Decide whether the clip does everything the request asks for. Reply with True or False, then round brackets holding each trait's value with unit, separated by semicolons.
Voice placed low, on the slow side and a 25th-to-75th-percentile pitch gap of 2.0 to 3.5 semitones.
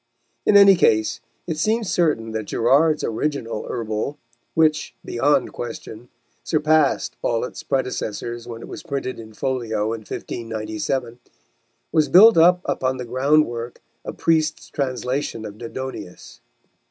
False (130 Hz; 130 wpm; 5.1 semitones)